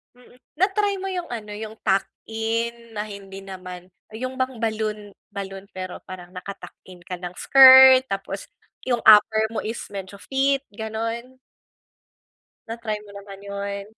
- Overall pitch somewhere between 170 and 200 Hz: No, high, 215 Hz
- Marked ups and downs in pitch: No, average, 3.7 semitones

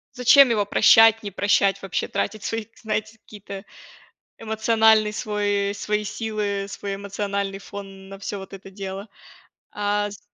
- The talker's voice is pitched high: Yes, high, 205 Hz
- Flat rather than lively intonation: Yes, narrow, 1.6 semitones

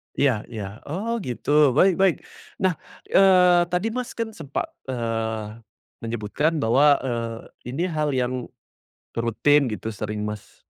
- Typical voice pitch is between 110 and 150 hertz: Yes, low, 135 Hz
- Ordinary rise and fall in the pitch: No, wide, 7.5 semitones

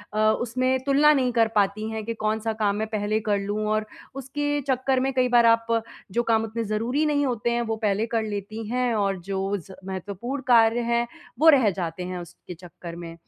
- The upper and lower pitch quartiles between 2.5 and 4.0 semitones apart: Yes, average, 3.6 semitones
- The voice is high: Yes, high, 225 Hz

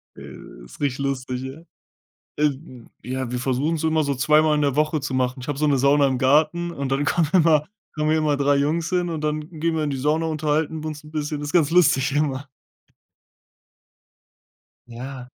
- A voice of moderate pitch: Yes, medium, 145 Hz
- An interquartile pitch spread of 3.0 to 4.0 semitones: No, narrow, 2.6 semitones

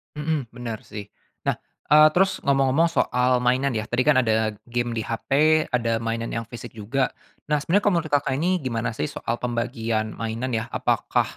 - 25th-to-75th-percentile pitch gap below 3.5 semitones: No, average, 4.0 semitones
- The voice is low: Yes, low, 125 Hz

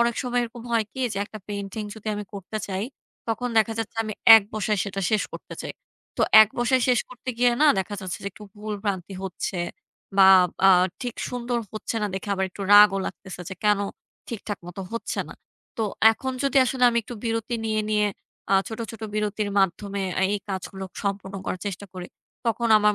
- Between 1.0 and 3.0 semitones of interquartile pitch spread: Yes, average, 2.7 semitones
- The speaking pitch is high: Yes, high, 210 Hz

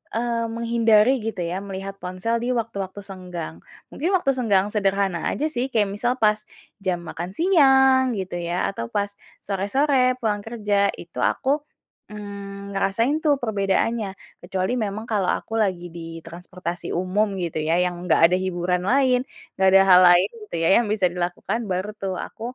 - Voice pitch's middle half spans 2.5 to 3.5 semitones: No, average, 3.9 semitones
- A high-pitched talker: Yes, high, 200 Hz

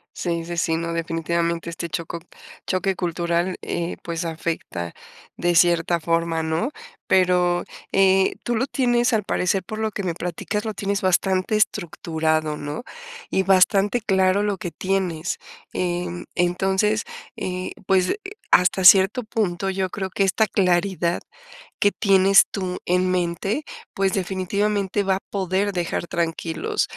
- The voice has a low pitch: No, medium, 185 Hz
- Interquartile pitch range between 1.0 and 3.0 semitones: Yes, narrow, 2.4 semitones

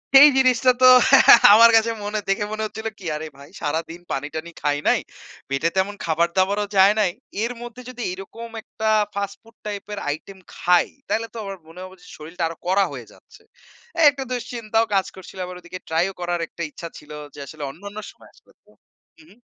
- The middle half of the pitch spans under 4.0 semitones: No, average, 4.4 semitones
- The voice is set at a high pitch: Yes, high, 195 Hz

